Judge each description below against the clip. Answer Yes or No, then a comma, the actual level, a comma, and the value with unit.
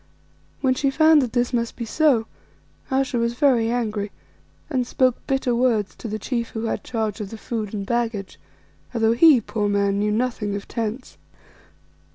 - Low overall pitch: No, high, 235 Hz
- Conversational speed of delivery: Yes, average, 175 wpm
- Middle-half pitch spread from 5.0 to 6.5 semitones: No, average, 3.0 semitones